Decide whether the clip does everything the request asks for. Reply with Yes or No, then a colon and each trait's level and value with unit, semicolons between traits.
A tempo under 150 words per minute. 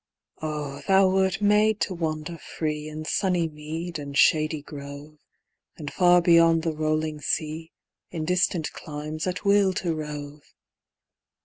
Yes: slow, 135 wpm